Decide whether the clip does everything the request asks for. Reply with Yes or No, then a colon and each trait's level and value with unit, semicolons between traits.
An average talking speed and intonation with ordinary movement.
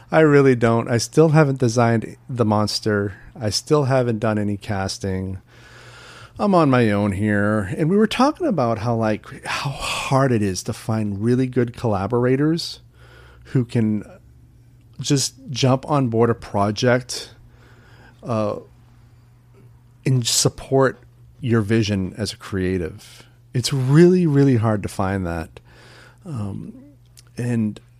No: slow, 130 wpm; average, 3.5 semitones